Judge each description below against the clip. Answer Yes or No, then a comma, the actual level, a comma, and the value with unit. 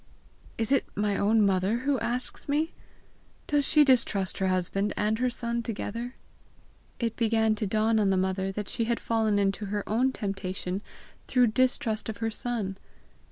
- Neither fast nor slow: Yes, average, 160 wpm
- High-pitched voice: Yes, high, 220 Hz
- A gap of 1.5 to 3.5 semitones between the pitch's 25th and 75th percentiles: Yes, average, 3.1 semitones